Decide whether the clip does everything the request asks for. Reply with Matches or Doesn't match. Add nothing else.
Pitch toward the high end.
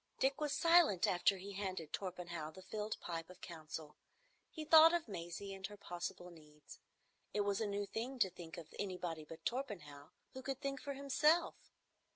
Matches